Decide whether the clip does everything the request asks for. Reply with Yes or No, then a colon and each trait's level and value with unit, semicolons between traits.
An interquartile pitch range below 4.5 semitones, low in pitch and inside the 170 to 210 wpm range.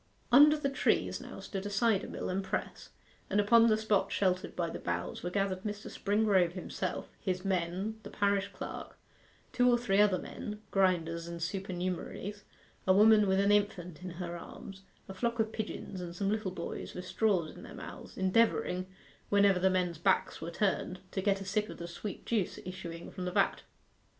No: narrow, 2.5 semitones; high, 195 Hz; average, 190 wpm